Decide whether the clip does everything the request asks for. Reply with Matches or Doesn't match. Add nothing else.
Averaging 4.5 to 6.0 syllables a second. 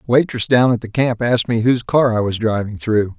Matches